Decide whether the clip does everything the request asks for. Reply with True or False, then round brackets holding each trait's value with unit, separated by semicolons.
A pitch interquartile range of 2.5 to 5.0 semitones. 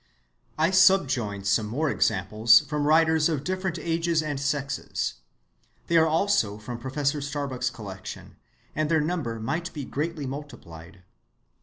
False (5.6 semitones)